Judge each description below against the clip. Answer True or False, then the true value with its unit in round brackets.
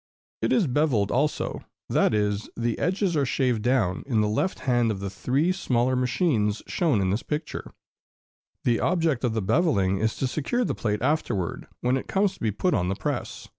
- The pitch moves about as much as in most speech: False (6.5 semitones)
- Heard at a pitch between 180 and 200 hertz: False (125 Hz)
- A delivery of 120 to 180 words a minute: False (195 wpm)